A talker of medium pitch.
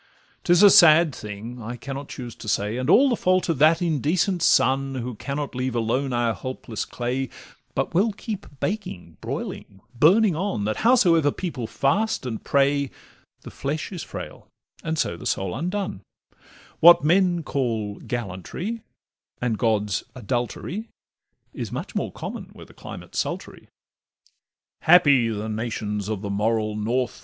No: low, 130 Hz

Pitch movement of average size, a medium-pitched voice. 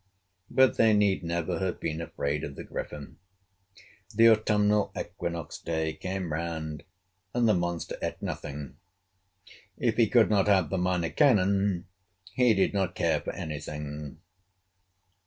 No: average, 4.5 semitones; very low, 90 Hz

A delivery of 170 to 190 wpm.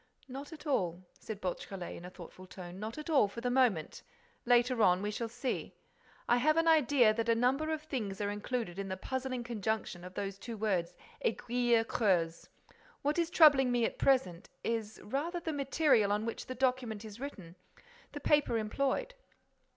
Yes: average, 175 wpm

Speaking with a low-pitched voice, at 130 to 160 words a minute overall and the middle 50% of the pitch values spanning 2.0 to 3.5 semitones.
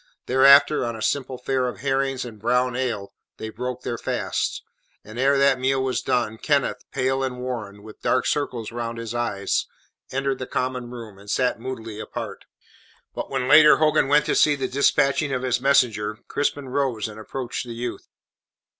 No: low, 125 Hz; average, 180 wpm; average, 2.7 semitones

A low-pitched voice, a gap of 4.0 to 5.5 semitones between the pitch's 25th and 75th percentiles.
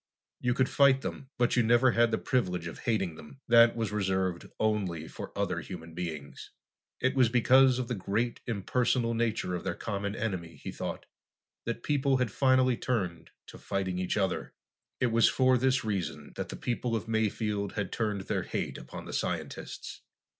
Yes: low, 110 Hz; average, 4.6 semitones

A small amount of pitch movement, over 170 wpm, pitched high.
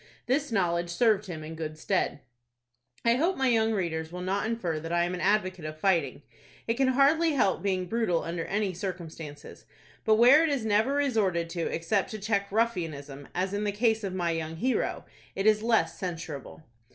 No: average, 5.1 semitones; average, 190 wpm; high, 195 Hz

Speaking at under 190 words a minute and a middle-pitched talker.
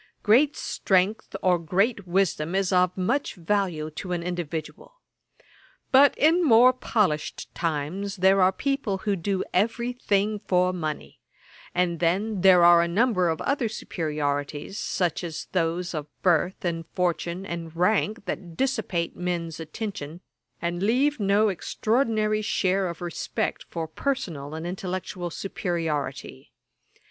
Yes: slow, 135 wpm; medium, 180 Hz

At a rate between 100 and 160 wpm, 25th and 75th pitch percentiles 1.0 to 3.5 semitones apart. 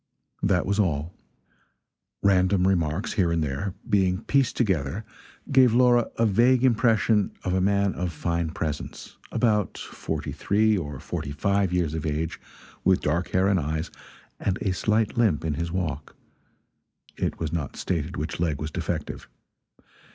No: average, 150 wpm; average, 4.4 semitones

